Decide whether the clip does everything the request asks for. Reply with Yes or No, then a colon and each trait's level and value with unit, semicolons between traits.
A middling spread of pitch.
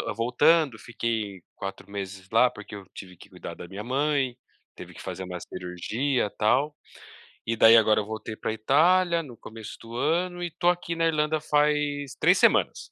No: wide, 6.3 semitones